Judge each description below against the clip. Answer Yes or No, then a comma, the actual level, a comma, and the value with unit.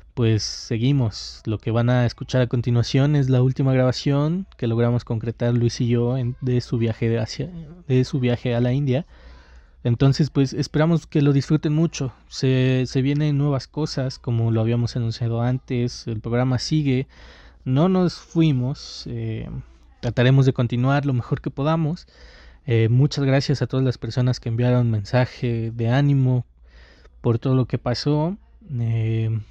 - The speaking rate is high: No, average, 165 wpm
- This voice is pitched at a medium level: No, low, 125 Hz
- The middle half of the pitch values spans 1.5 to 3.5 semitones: Yes, average, 3.0 semitones